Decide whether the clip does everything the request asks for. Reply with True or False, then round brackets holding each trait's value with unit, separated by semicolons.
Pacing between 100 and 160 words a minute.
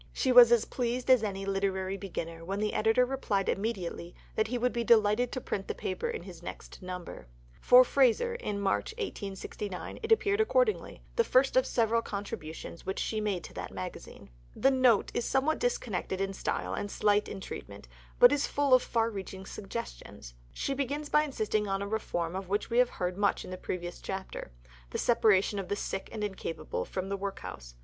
False (195 wpm)